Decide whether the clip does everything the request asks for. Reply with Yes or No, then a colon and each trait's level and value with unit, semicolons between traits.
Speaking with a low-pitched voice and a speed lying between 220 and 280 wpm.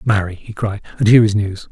Yes: low, 105 Hz; fast, 245 wpm